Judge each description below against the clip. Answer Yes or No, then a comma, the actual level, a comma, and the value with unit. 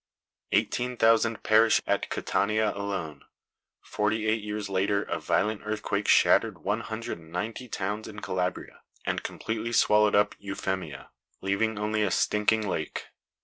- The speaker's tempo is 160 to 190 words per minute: No, average, 140 wpm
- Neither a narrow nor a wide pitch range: No, narrow, 1.9 semitones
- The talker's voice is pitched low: Yes, low, 105 Hz